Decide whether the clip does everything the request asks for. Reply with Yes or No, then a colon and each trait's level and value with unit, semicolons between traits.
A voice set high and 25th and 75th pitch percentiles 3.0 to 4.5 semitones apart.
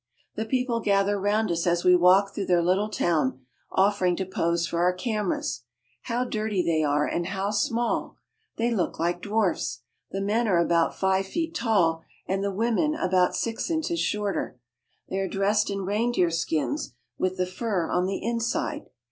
Yes: high, 195 Hz; average, 3.8 semitones